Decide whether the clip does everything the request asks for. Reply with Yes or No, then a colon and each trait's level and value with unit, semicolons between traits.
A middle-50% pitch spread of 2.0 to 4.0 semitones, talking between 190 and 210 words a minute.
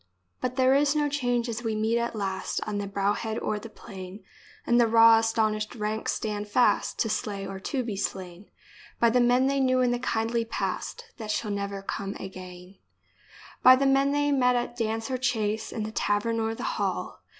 Yes: average, 3.2 semitones; fast, 205 wpm